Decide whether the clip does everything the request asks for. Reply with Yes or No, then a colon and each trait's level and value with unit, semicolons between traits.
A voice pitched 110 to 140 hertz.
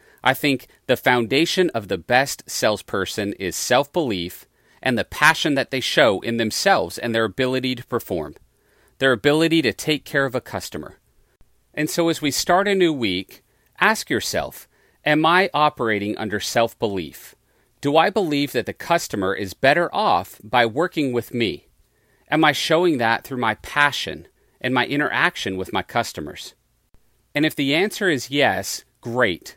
Yes: low, 135 Hz